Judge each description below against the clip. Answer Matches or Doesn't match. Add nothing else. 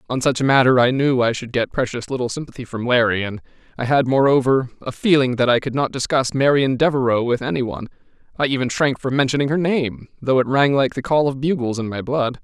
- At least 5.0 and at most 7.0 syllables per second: Matches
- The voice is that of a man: Matches